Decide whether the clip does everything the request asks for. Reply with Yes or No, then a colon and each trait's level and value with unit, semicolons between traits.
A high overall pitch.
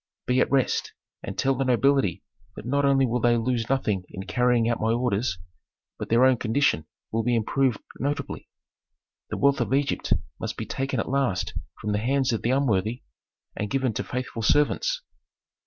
No: low, 125 Hz